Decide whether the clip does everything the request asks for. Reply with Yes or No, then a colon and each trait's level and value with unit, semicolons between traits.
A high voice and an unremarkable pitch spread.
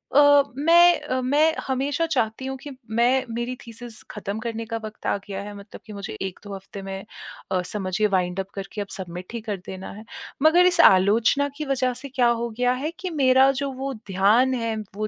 Yes: high, 230 Hz; average, 5.0 semitones